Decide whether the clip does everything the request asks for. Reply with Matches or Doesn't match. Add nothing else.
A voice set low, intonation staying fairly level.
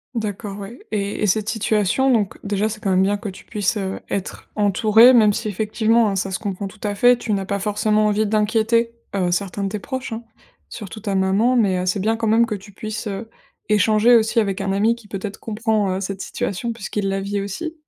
Doesn't match